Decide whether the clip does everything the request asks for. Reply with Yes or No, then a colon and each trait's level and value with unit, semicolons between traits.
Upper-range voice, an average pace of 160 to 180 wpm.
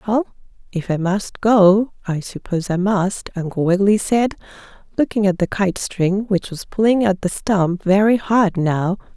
Yes: high, 195 Hz; average, 170 wpm